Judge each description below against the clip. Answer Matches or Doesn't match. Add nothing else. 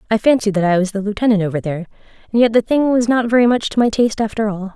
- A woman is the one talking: Matches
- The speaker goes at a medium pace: Doesn't match